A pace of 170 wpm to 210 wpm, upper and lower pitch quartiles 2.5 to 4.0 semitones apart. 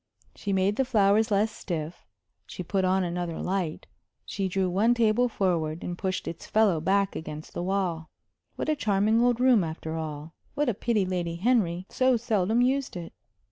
No: average, 180 wpm; average, 4.4 semitones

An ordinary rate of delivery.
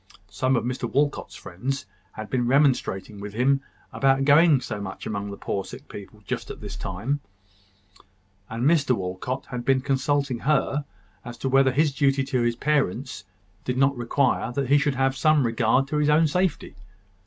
Yes: average, 175 wpm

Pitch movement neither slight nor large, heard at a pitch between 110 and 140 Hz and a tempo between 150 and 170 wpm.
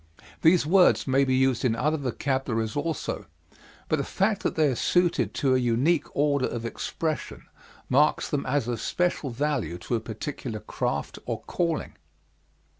Yes: average, 4.3 semitones; low, 135 Hz; average, 160 wpm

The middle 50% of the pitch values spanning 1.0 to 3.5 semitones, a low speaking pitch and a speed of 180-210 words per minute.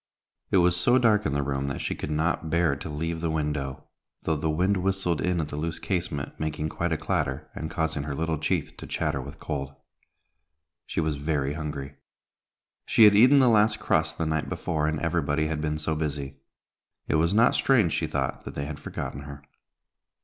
Yes: average, 2.9 semitones; very low, 80 Hz; average, 200 wpm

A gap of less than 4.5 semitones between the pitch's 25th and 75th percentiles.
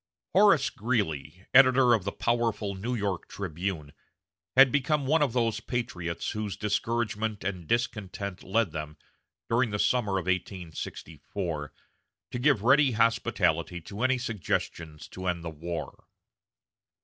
No: average, 5.3 semitones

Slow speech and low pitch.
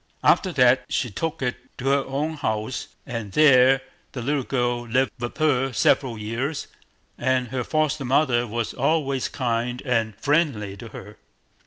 No: average, 155 wpm; low, 125 Hz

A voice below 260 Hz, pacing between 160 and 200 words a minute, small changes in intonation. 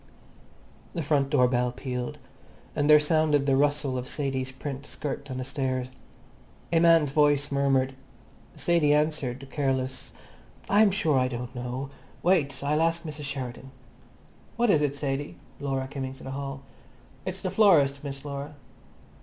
No: medium, 140 Hz; average, 150 wpm; narrow, 2.1 semitones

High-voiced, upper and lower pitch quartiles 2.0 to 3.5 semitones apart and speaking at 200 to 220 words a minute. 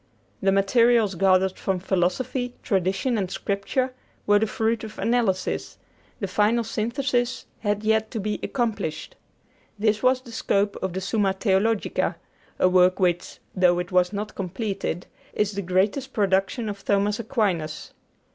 No: high, 205 Hz; average, 3.1 semitones; average, 145 wpm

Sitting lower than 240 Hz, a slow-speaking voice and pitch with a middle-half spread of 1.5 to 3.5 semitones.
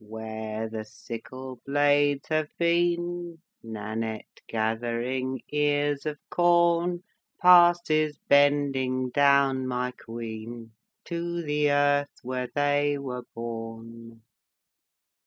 No: low, 135 Hz; slow, 90 wpm; average, 4.3 semitones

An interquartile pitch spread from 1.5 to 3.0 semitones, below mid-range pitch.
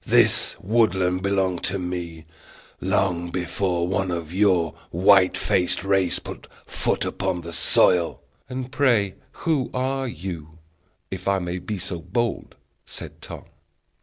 Yes: narrow, 2.4 semitones; very low, 95 Hz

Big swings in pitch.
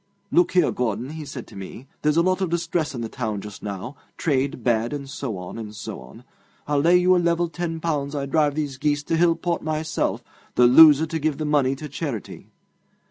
No: average, 4.5 semitones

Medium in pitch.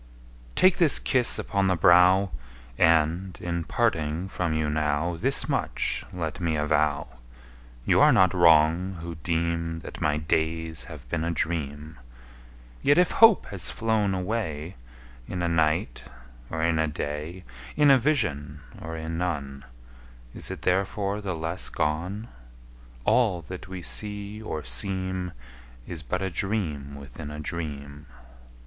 No: very low, 85 Hz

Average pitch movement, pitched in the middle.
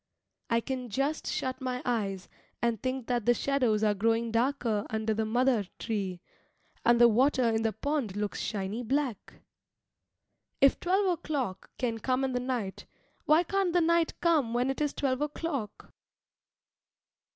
No: average, 3.9 semitones; high, 245 Hz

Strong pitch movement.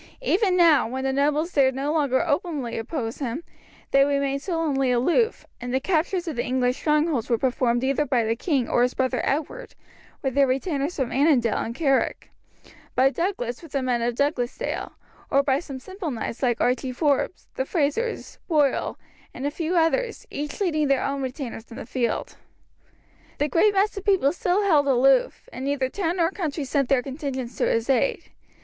No: average, 4.2 semitones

